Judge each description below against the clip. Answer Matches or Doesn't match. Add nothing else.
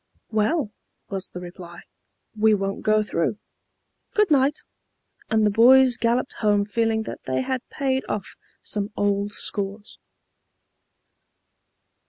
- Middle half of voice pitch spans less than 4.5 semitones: Matches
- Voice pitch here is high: Matches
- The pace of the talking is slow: Matches